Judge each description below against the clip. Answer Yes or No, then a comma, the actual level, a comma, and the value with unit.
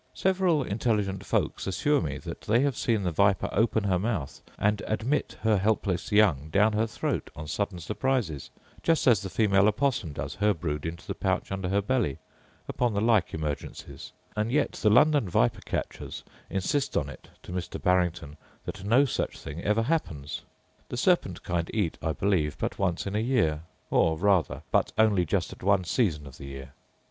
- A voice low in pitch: Yes, low, 100 Hz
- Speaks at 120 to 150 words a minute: No, average, 185 wpm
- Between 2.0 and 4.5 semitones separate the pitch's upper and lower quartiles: No, average, 5.1 semitones